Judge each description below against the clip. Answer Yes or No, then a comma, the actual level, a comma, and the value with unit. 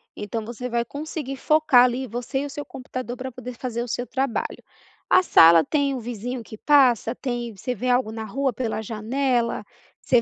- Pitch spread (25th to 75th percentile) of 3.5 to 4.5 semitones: No, narrow, 2.5 semitones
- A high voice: Yes, high, 245 Hz